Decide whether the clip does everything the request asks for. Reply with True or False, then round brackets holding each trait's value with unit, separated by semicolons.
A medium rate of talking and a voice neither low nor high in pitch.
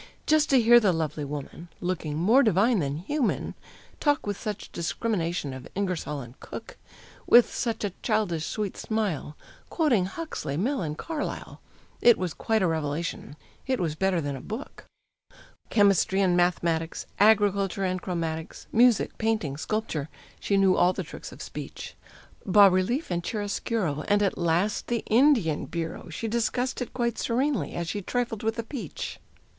False (160 wpm; 195 Hz)